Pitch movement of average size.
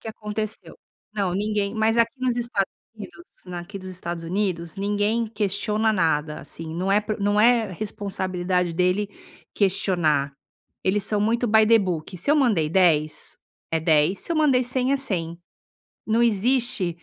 Yes: average, 3.9 semitones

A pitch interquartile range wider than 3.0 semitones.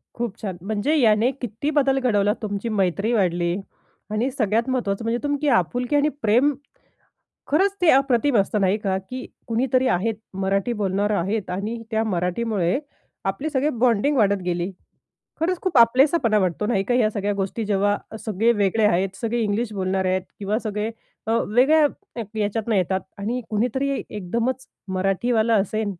Yes: average, 3.9 semitones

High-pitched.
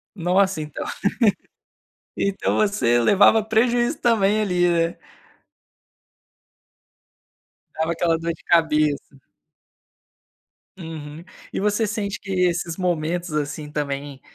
No: medium, 175 Hz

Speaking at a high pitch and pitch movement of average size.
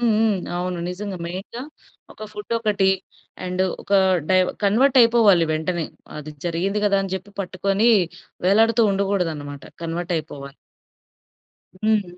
Yes: high, 195 Hz; average, 3.4 semitones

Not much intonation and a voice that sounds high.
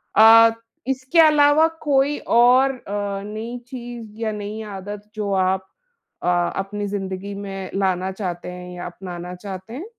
No: average, 4.1 semitones; high, 205 Hz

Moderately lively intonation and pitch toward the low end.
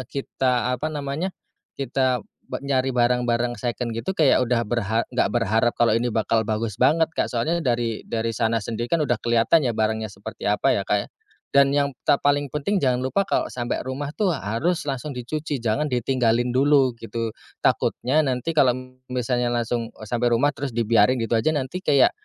Yes: average, 3.3 semitones; low, 125 Hz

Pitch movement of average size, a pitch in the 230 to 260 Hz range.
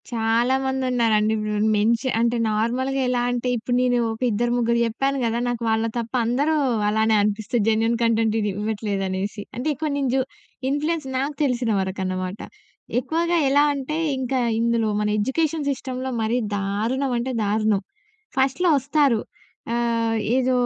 Yes: average, 3.3 semitones; high, 235 Hz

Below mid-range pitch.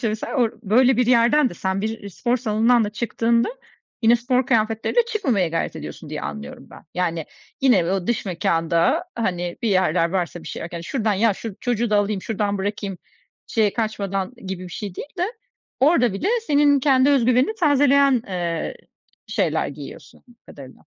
No: high, 220 Hz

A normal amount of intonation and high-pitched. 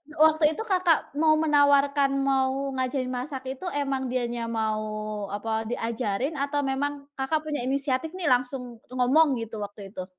Yes: average, 3.0 semitones; very high, 270 Hz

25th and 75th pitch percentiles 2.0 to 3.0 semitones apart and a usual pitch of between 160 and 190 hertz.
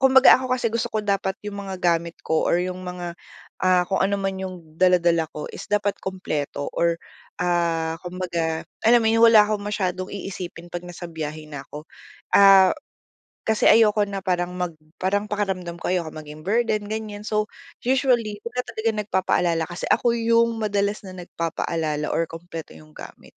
No: average, 3.7 semitones; medium, 185 Hz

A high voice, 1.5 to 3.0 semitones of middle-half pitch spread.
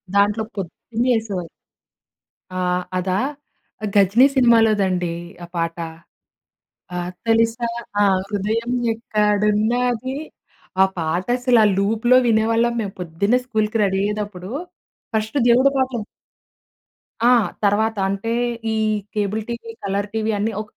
Yes: high, 215 Hz; narrow, 2.6 semitones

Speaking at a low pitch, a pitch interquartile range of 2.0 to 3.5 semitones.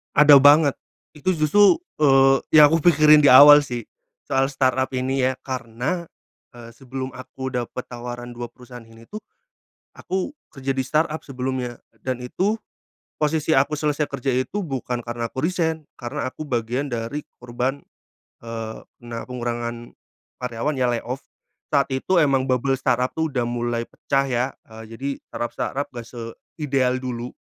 Yes: low, 130 Hz; average, 3.2 semitones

